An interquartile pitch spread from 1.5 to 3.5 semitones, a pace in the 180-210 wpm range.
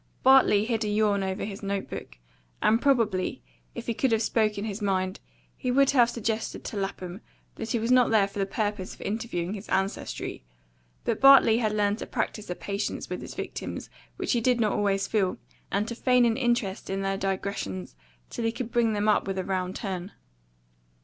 Yes: average, 2.9 semitones; average, 200 wpm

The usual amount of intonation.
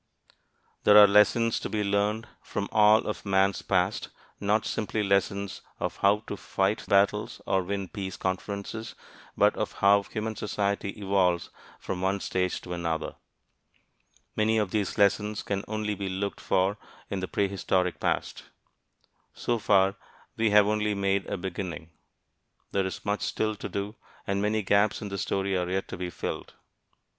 No: narrow, 1.6 semitones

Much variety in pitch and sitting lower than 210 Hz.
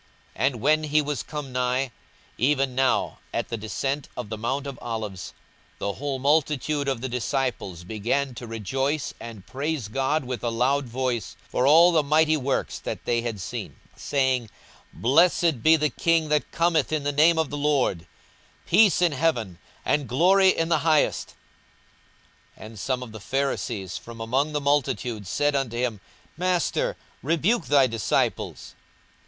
No: average, 4.3 semitones; low, 135 Hz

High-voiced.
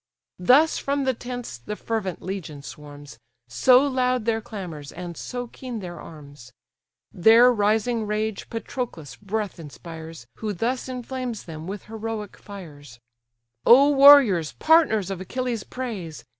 Yes: high, 210 Hz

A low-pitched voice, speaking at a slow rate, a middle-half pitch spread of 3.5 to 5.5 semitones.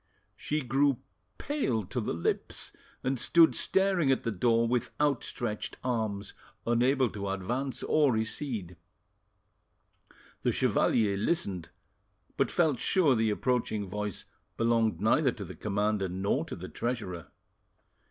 Yes: low, 115 Hz; slow, 125 wpm; average, 4.5 semitones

